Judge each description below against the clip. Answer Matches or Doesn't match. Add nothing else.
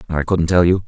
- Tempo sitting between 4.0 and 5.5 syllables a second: Doesn't match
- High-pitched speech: Doesn't match